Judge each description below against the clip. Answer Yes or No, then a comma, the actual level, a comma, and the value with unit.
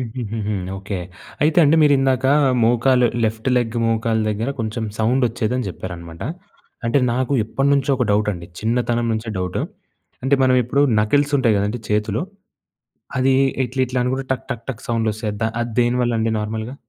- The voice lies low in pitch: Yes, low, 115 Hz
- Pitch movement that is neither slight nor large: Yes, average, 3.0 semitones